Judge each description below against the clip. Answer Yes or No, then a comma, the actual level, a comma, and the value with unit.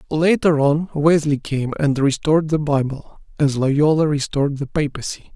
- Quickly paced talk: No, average, 145 wpm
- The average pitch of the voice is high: No, medium, 145 Hz